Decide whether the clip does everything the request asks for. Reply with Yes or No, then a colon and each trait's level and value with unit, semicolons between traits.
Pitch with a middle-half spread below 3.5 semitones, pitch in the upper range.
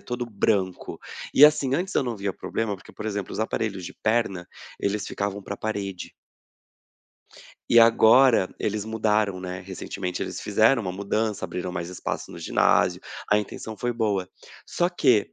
No: average, 2.9 semitones; low, 105 Hz